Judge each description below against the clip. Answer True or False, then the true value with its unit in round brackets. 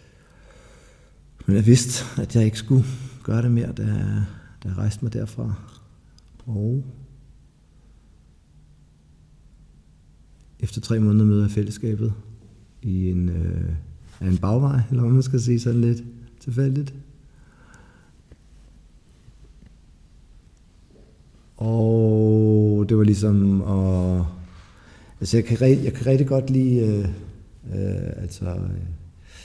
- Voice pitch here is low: True (105 Hz)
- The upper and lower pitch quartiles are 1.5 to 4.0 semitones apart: False (4.9 semitones)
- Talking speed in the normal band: False (110 wpm)